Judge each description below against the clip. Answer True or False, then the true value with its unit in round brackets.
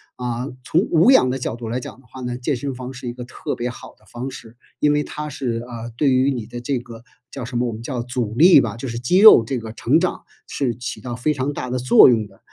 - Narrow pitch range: True (2.3 semitones)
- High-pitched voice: False (125 Hz)